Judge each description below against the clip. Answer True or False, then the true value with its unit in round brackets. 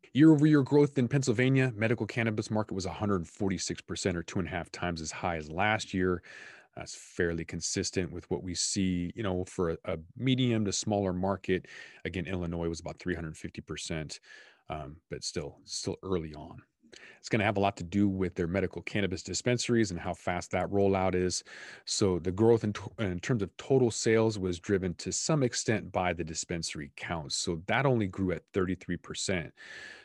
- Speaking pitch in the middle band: False (95 Hz)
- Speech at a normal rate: True (190 wpm)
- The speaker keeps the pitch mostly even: False (4.4 semitones)